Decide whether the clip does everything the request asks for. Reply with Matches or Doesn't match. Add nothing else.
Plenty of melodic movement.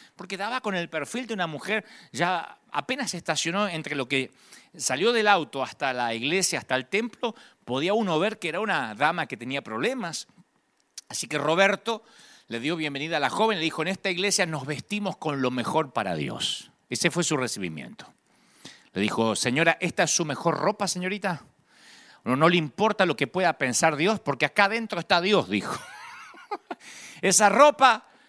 Matches